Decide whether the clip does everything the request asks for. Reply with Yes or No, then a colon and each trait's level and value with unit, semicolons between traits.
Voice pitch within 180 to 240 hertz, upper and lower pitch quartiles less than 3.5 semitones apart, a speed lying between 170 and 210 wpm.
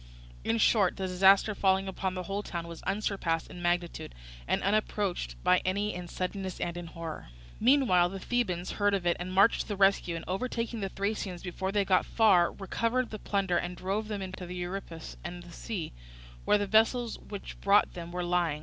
Yes: high, 190 Hz; narrow, 2.6 semitones; fast, 205 wpm